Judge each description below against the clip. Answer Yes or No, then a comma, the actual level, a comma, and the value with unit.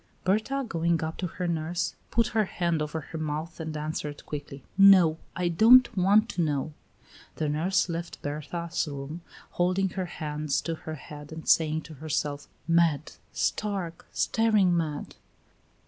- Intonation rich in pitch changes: No, average, 3.1 semitones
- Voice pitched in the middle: Yes, medium, 165 Hz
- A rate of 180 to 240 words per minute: No, average, 150 wpm